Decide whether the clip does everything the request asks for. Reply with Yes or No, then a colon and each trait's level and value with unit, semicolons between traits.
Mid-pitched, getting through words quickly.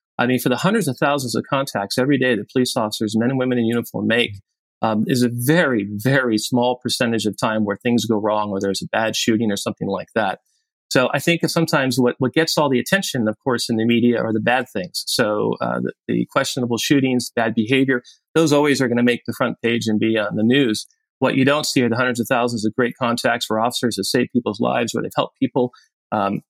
No: low, 120 Hz; fast, 240 wpm